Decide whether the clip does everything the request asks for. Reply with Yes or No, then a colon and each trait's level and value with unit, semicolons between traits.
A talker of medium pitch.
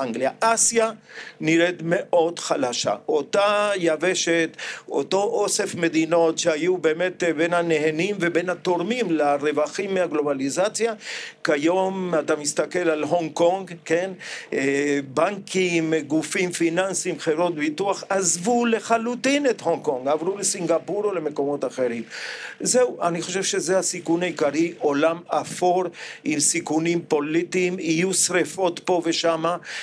Yes: medium, 170 Hz